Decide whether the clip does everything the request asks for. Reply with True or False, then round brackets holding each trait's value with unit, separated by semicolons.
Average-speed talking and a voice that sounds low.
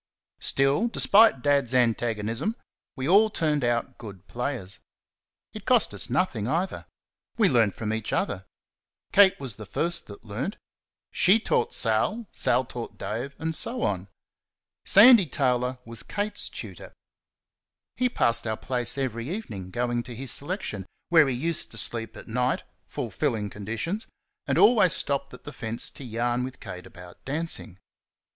True (150 wpm; 125 Hz)